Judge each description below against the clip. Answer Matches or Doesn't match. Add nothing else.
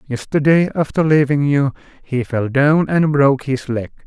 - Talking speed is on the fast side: Doesn't match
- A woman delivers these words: Doesn't match